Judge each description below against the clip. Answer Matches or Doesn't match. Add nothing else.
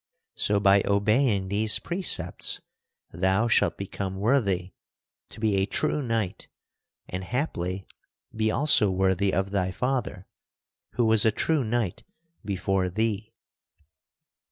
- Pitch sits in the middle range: Doesn't match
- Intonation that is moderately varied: Matches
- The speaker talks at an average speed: Doesn't match